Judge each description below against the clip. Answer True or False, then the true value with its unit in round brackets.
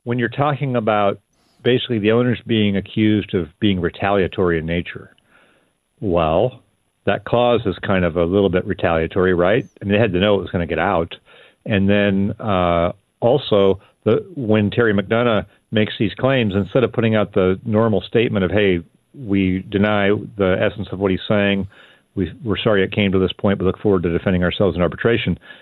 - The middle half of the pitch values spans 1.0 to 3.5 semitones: True (2.9 semitones)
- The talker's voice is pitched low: True (100 Hz)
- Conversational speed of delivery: True (190 wpm)